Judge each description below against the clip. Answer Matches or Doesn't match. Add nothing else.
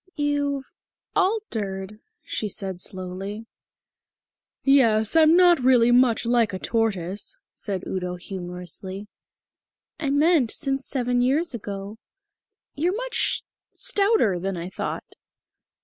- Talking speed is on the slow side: Matches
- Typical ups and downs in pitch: Doesn't match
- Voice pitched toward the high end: Matches